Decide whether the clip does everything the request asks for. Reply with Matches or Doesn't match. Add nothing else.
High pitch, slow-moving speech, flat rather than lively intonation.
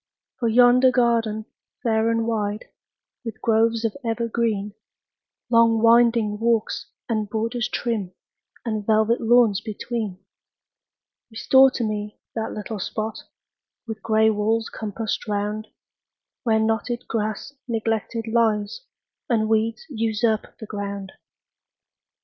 Matches